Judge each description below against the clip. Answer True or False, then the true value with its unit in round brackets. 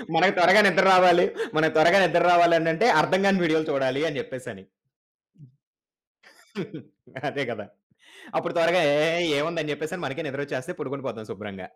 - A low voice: False (160 Hz)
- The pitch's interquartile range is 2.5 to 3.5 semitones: False (4.3 semitones)